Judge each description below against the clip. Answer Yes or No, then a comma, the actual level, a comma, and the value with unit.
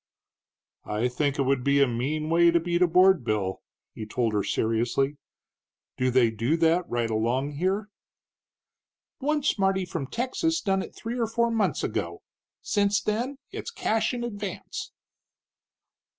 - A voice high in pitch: No, medium, 165 Hz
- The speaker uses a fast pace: No, average, 150 wpm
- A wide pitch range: Yes, wide, 8.9 semitones